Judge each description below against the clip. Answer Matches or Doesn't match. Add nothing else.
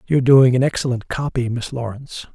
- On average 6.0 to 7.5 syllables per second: Matches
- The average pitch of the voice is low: Matches